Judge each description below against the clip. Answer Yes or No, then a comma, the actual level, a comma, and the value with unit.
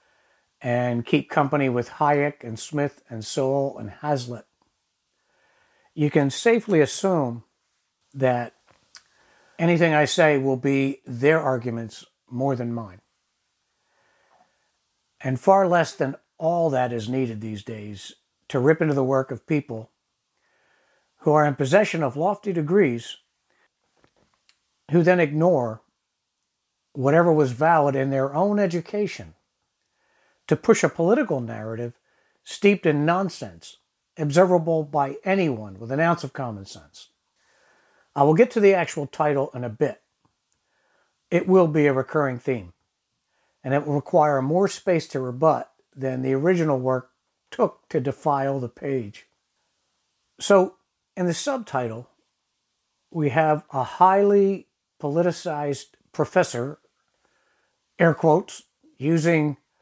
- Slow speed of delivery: Yes, slow, 125 wpm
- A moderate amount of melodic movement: Yes, average, 4.9 semitones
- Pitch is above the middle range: No, medium, 145 Hz